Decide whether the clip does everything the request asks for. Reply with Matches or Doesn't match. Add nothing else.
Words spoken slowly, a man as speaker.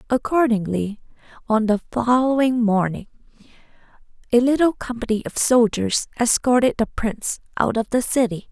Doesn't match